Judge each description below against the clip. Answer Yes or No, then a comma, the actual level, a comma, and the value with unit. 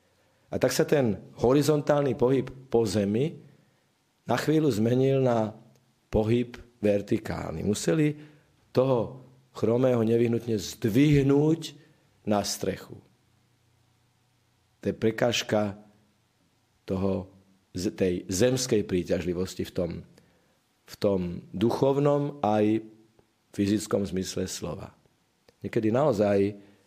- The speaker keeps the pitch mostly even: No, average, 3.8 semitones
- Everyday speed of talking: No, slow, 85 wpm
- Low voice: Yes, low, 115 Hz